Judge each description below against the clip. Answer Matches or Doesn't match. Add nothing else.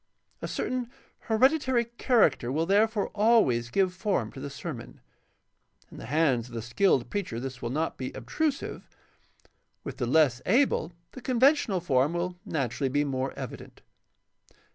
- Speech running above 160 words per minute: Doesn't match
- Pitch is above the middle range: Doesn't match